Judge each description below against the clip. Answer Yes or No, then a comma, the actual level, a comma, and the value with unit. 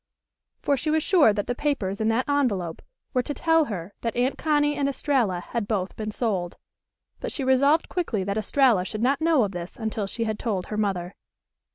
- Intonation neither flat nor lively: No, wide, 5.9 semitones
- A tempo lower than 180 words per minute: No, fast, 205 wpm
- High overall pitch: Yes, high, 230 Hz